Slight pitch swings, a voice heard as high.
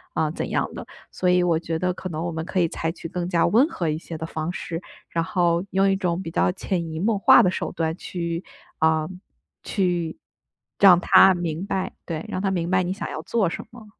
No: narrow, 2.2 semitones; medium, 175 Hz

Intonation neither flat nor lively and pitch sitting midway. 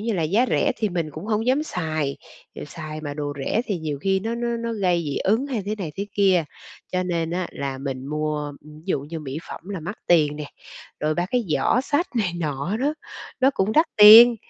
No: wide, 6.3 semitones; medium, 180 Hz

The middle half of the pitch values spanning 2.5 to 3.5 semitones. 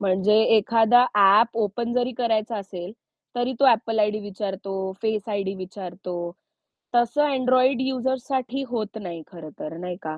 No: average, 4.0 semitones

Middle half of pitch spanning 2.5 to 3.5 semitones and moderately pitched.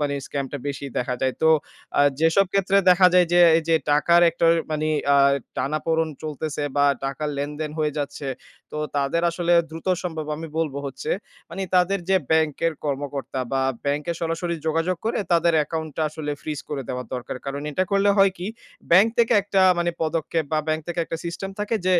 Yes: average, 2.9 semitones; medium, 160 Hz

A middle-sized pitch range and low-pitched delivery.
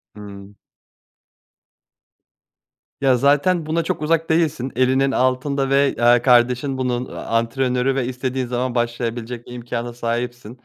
No: narrow, 2.2 semitones; low, 125 Hz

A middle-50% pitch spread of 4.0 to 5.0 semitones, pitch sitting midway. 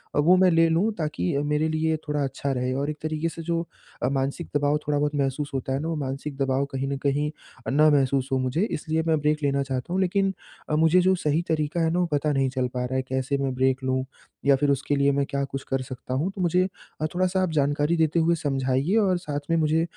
No: average, 3.1 semitones; medium, 145 Hz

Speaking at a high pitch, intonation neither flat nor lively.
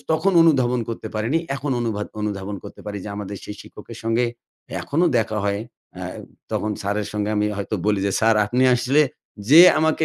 No: low, 110 Hz; average, 4.3 semitones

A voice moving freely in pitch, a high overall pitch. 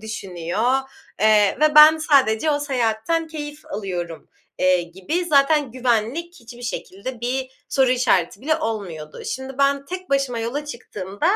Yes: wide, 5.8 semitones; very high, 250 Hz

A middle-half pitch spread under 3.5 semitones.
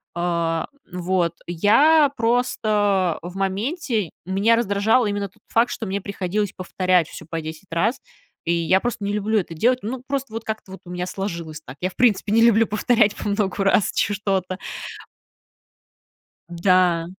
No: average, 3.9 semitones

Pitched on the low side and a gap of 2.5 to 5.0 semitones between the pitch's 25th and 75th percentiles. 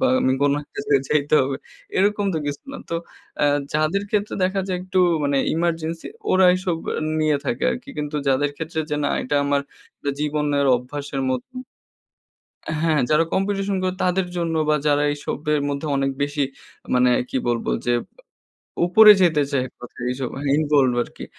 No: medium, 150 Hz; average, 4.0 semitones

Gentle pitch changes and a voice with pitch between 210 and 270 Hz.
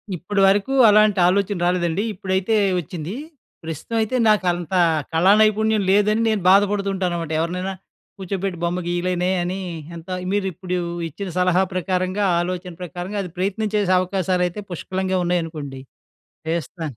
No: narrow, 2.3 semitones; medium, 185 Hz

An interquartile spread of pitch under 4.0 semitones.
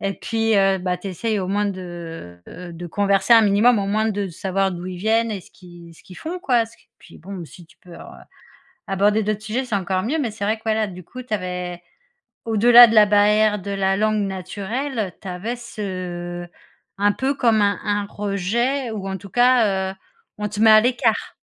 Yes: average, 3.0 semitones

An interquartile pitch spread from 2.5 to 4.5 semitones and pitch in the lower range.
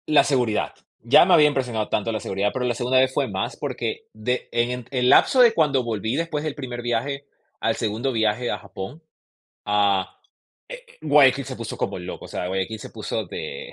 No: average, 4.9 semitones; low, 125 Hz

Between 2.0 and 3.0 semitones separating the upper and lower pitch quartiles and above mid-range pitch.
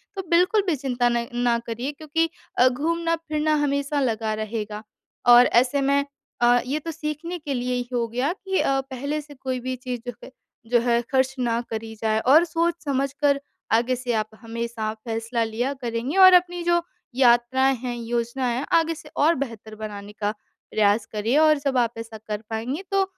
No: average, 4.4 semitones; very high, 255 Hz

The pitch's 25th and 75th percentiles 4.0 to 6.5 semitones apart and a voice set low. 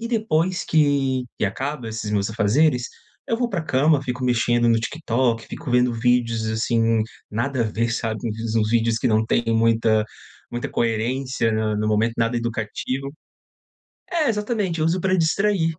Yes: average, 5.3 semitones; low, 120 Hz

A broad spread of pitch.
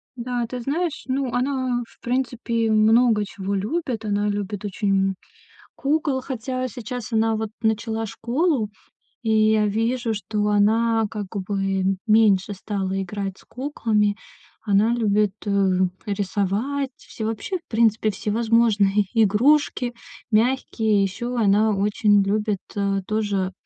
No: average, 3.0 semitones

